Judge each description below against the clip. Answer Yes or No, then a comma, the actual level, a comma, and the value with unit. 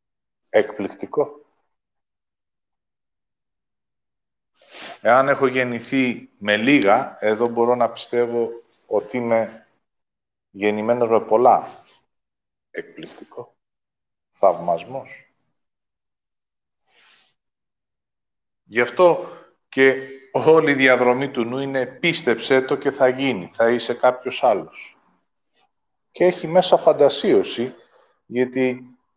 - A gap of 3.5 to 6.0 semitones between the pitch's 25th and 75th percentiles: No, average, 2.7 semitones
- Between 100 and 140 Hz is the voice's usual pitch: Yes, low, 125 Hz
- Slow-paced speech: Yes, slow, 80 wpm